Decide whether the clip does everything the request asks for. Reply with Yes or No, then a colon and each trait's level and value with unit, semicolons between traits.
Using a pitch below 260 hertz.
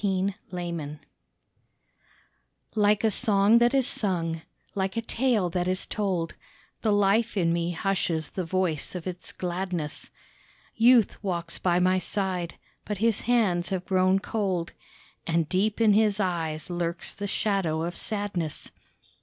Yes: medium, 185 Hz